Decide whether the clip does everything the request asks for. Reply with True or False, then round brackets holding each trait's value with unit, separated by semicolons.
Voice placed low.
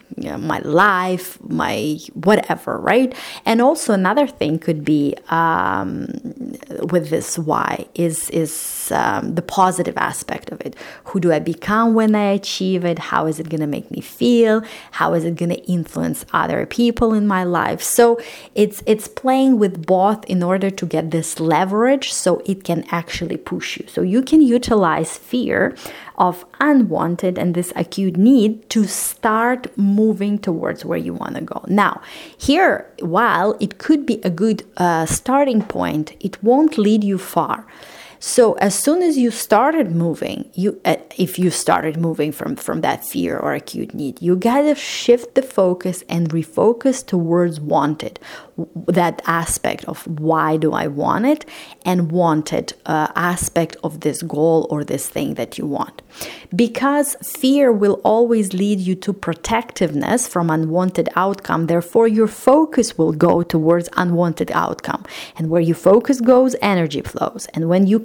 False (185 Hz)